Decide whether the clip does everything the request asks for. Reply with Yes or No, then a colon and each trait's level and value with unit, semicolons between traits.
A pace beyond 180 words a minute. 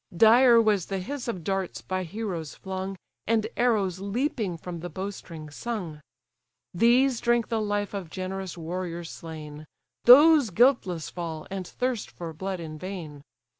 No: average, 150 wpm